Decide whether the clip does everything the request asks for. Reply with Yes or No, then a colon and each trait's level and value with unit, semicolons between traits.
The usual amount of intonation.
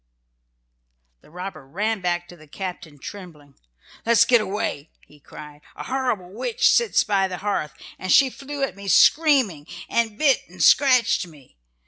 No: wide, 6.4 semitones